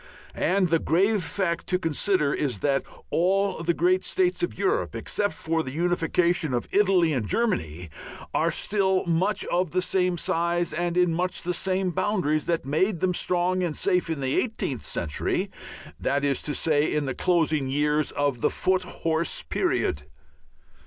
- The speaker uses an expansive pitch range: No, average, 3.7 semitones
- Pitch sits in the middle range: Yes, medium, 170 Hz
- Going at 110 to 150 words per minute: No, average, 165 wpm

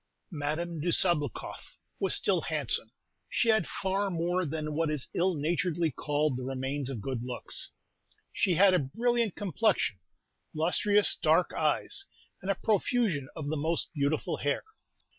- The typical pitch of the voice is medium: Yes, medium, 165 Hz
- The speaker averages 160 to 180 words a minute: No, average, 145 wpm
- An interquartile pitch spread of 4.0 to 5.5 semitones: Yes, average, 4.7 semitones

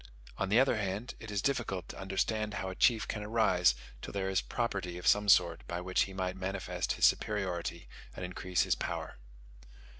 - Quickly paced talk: No, average, 190 wpm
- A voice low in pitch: Yes, very low, 95 Hz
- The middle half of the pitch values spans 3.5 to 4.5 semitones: No, narrow, 2.6 semitones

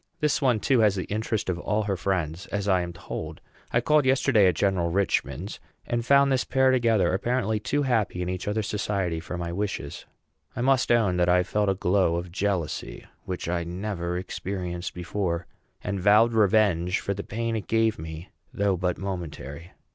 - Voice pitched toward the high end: No, low, 100 Hz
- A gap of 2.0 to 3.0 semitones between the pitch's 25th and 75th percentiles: No, average, 3.9 semitones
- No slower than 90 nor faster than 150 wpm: No, average, 185 wpm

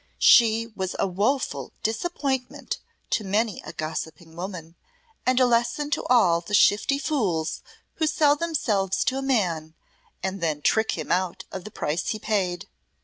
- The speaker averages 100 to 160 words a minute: Yes, average, 155 wpm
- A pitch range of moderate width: No, wide, 6.4 semitones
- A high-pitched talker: Yes, high, 210 Hz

